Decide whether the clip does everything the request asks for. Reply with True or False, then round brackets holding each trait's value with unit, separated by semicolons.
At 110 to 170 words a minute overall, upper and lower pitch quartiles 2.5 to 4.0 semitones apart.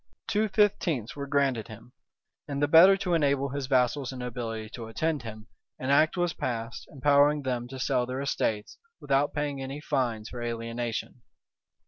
True (165 wpm; 3.5 semitones)